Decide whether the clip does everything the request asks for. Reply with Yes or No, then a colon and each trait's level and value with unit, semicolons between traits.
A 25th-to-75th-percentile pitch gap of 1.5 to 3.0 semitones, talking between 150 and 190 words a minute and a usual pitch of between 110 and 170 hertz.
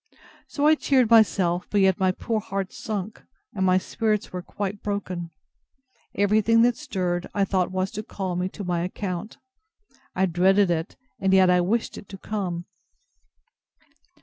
No: average, 2.7 semitones; average, 160 wpm; high, 190 Hz